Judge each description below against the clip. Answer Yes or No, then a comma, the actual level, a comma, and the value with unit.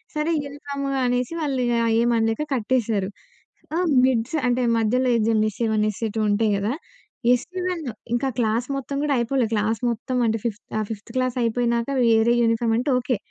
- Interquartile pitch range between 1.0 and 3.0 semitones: Yes, narrow, 2.5 semitones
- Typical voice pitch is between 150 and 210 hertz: No, high, 235 Hz